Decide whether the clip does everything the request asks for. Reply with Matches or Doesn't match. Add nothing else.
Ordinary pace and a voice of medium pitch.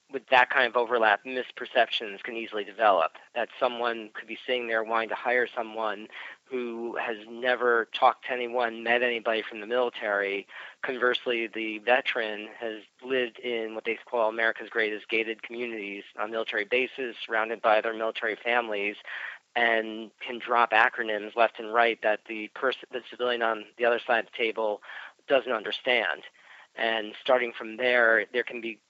Doesn't match